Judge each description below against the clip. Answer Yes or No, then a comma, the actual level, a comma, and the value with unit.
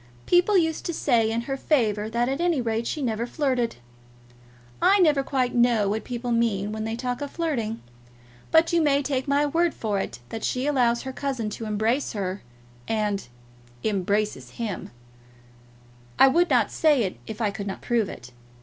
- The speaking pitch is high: Yes, high, 240 Hz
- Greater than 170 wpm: Yes, average, 180 wpm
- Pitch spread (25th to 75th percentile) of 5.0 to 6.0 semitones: No, average, 4.6 semitones